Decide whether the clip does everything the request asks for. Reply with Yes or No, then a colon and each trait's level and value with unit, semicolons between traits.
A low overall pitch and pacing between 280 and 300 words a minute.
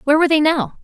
No: very high, 295 Hz; fast, 285 wpm